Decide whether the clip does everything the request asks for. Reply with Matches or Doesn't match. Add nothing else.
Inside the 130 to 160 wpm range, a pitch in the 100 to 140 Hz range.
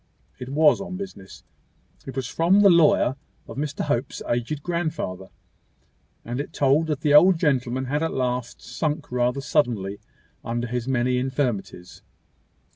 Matches